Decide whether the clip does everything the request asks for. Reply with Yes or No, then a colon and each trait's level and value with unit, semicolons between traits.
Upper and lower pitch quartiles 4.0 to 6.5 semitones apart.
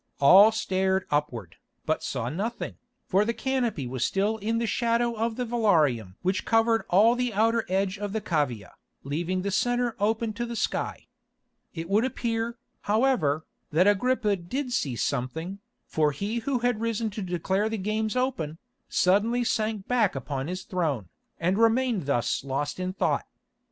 Yes: wide, 5.5 semitones